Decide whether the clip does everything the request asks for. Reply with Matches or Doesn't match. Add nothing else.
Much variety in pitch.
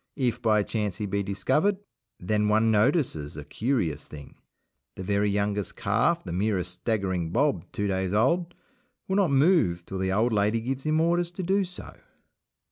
Matches